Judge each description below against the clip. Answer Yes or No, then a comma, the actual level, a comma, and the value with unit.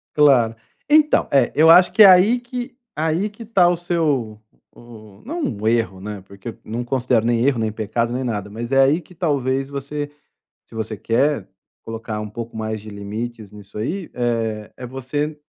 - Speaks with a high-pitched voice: No, low, 125 Hz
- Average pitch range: No, wide, 6.0 semitones